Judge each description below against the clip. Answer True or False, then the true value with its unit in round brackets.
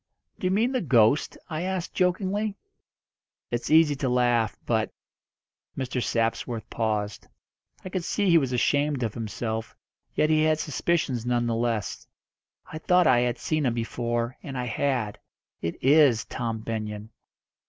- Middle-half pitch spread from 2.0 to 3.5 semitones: False (5.4 semitones)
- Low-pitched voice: True (125 Hz)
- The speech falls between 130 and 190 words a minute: True (155 wpm)